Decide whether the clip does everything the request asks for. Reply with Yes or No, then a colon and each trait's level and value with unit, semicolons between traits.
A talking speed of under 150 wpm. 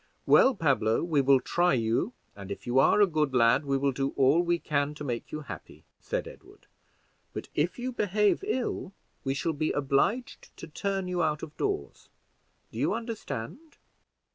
No: average, 180 wpm